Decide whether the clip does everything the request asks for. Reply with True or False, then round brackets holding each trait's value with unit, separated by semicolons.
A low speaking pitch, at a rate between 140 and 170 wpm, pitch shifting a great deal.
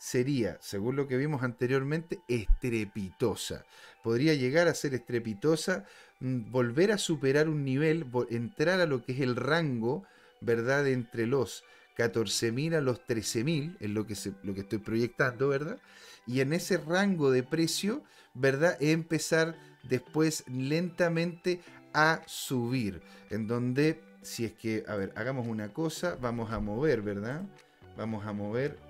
True (130 Hz; 145 wpm; 5.7 semitones)